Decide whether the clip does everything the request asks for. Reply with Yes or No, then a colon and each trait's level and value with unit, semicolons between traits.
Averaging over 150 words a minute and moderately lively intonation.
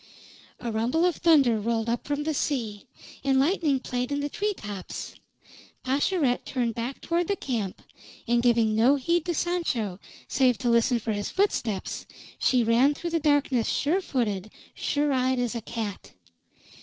Yes: average, 165 wpm; average, 4.3 semitones